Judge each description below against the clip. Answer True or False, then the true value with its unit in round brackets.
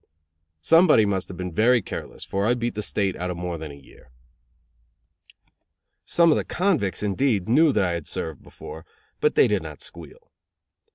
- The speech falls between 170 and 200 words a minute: True (180 wpm)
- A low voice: True (100 Hz)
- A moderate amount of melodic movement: False (6.9 semitones)